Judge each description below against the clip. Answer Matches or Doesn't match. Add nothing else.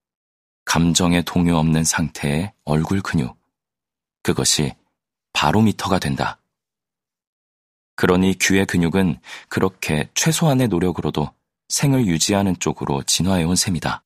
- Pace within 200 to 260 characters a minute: Matches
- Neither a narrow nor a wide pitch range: Matches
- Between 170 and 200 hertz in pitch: Doesn't match